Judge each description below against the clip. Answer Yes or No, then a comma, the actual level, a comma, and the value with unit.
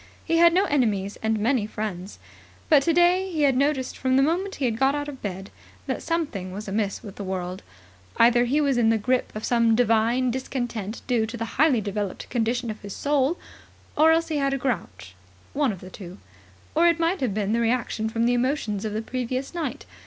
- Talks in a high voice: Yes, high, 245 Hz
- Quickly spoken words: Yes, fast, 210 wpm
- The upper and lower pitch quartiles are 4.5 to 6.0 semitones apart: Yes, average, 4.9 semitones